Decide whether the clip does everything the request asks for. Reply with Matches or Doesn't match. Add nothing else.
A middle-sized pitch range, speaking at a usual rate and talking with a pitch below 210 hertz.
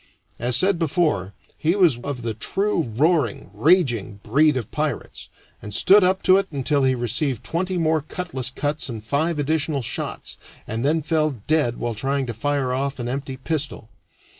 Matches